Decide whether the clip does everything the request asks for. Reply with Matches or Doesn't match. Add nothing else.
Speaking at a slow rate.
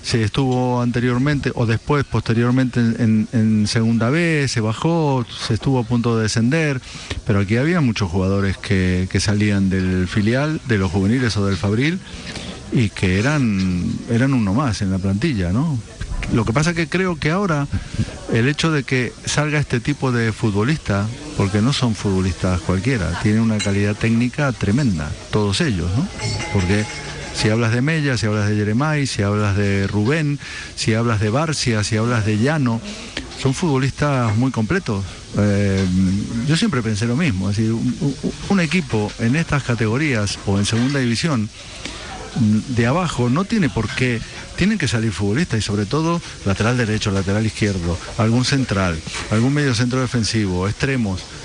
Doesn't match